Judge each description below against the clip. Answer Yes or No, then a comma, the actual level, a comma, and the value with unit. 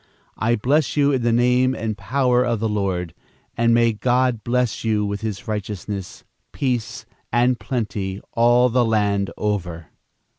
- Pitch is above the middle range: No, low, 115 Hz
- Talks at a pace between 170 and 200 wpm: No, average, 150 wpm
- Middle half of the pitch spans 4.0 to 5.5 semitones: No, average, 3.2 semitones